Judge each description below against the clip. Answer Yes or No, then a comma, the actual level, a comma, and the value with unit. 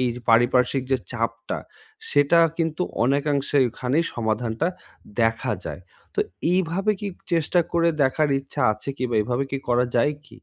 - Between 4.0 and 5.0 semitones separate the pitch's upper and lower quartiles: Yes, average, 4.6 semitones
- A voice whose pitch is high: No, low, 135 Hz